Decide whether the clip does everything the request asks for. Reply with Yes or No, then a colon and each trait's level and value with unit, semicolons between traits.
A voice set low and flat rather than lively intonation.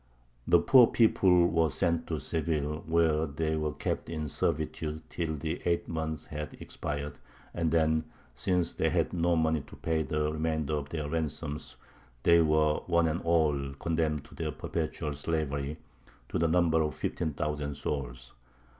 Yes: very low, 80 Hz; narrow, 1.6 semitones